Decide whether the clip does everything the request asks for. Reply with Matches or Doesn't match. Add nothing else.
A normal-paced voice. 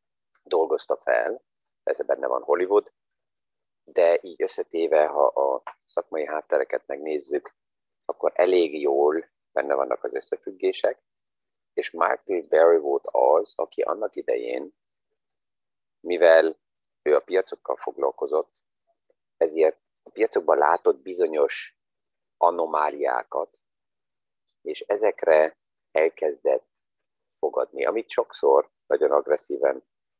Doesn't match